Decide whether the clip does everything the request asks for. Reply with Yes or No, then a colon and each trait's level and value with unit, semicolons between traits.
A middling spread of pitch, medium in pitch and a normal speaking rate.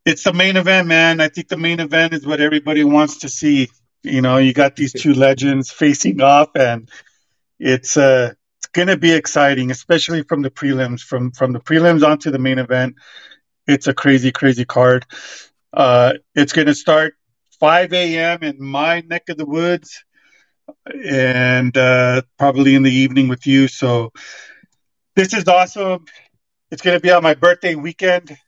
Yes: average, 4.0 semitones; medium, 145 Hz; average, 170 wpm